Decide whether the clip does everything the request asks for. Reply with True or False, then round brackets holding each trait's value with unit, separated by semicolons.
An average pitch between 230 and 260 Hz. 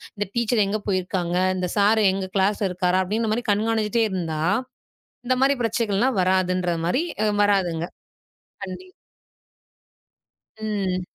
False (200 Hz)